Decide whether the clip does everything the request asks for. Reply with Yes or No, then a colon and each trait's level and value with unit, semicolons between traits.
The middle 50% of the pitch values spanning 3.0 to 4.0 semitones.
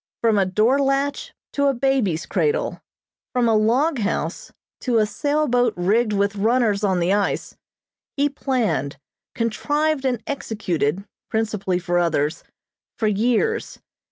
No: wide, 5.4 semitones